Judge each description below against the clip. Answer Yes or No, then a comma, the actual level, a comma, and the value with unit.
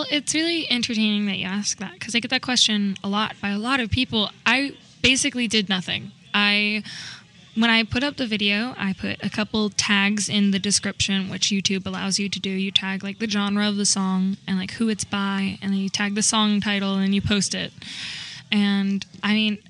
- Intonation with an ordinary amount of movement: No, narrow, 1.9 semitones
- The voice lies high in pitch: Yes, high, 205 Hz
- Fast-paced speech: Yes, fast, 215 wpm